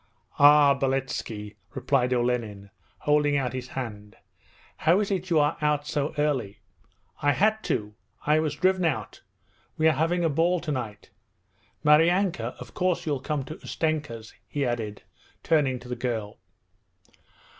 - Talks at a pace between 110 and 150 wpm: Yes, average, 145 wpm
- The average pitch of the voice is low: No, medium, 145 Hz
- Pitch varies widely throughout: No, average, 4.3 semitones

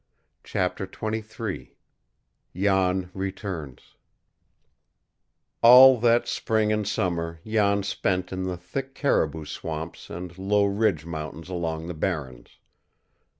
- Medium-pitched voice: No, very low, 95 Hz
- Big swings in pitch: No, average, 4.3 semitones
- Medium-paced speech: No, slow, 105 wpm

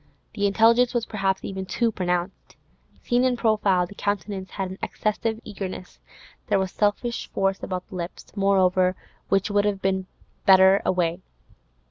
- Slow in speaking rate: No, average, 150 wpm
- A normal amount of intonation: No, narrow, 2.2 semitones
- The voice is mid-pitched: No, high, 195 Hz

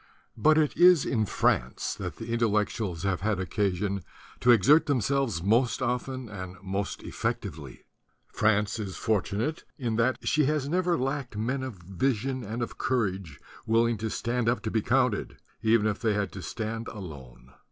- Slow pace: No, average, 165 wpm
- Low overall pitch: Yes, low, 110 Hz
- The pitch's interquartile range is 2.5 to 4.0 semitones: No, average, 4.5 semitones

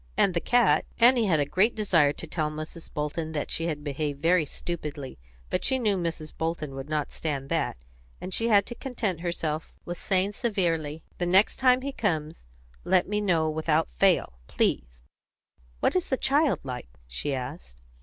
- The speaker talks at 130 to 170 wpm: No, average, 180 wpm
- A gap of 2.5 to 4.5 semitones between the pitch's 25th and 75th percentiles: No, average, 5.2 semitones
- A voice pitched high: No, medium, 165 Hz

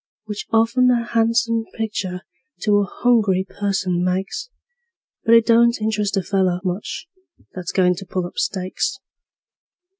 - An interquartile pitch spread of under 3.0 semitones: No, average, 3.5 semitones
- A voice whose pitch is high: Yes, high, 205 Hz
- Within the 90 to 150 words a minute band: Yes, average, 140 wpm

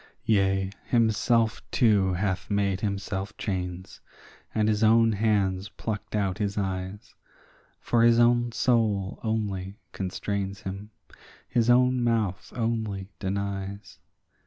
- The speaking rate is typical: No, slow, 110 wpm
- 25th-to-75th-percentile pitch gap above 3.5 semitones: No, average, 2.7 semitones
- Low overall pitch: Yes, low, 100 Hz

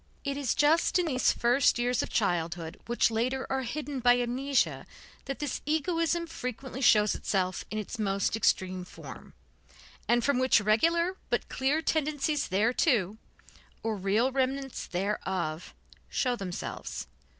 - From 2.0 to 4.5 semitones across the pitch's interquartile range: No, average, 5.1 semitones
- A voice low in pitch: No, high, 245 Hz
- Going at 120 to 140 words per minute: Yes, slow, 135 wpm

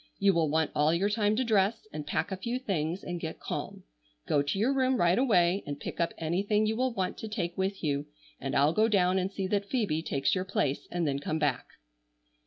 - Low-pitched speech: No, medium, 185 Hz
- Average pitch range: Yes, average, 4.9 semitones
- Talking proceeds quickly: Yes, fast, 230 wpm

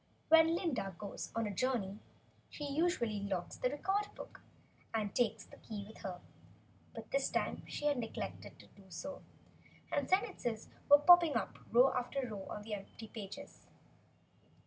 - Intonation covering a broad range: Yes, wide, 6.1 semitones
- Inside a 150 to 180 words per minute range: Yes, average, 160 wpm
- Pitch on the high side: Yes, high, 235 Hz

